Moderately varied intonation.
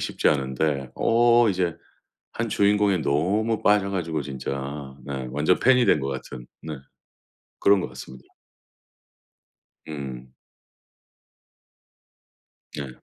No: wide, 6.9 semitones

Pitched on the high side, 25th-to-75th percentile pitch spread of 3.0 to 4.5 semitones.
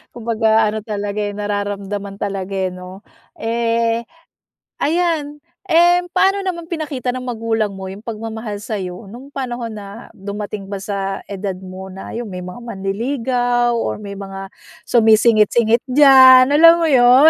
Yes: high, 220 Hz; average, 4.0 semitones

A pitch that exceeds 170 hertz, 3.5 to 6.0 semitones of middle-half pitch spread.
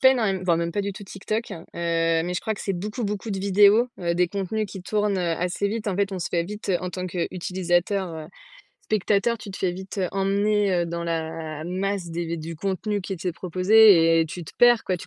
No: medium, 185 Hz; average, 3.1 semitones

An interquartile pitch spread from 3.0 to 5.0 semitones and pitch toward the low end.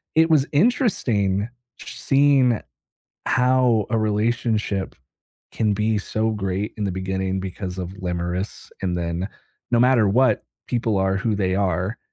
Yes: average, 4.1 semitones; low, 105 Hz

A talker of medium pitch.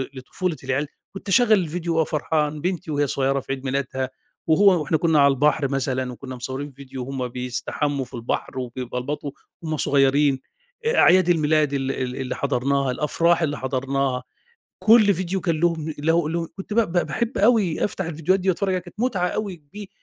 Yes: medium, 150 Hz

